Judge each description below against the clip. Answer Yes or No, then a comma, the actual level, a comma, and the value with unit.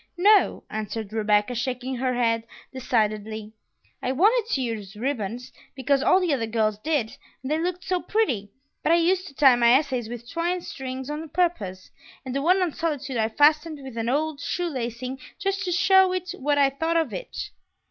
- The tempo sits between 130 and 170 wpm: No, average, 185 wpm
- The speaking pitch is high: Yes, very high, 270 Hz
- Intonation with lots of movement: Yes, wide, 6.3 semitones